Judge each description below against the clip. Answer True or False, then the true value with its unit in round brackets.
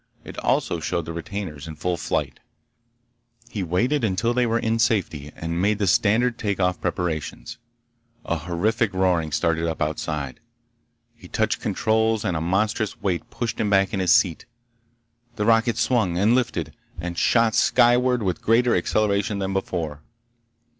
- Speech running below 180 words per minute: True (155 wpm)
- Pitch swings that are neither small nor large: True (4.9 semitones)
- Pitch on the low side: True (95 Hz)